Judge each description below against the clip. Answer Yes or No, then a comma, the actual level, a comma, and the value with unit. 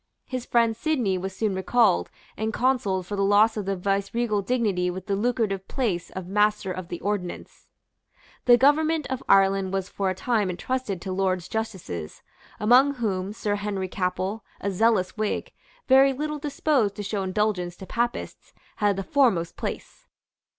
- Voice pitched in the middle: No, high, 205 Hz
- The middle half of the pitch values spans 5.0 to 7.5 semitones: No, average, 4.0 semitones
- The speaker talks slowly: No, average, 165 wpm